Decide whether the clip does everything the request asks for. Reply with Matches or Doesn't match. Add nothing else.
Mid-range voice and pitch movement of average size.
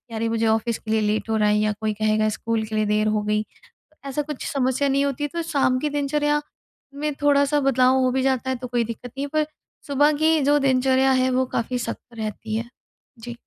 Doesn't match